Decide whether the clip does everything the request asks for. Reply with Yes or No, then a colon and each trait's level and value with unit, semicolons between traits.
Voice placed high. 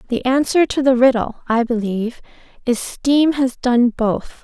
Yes: very high, 250 Hz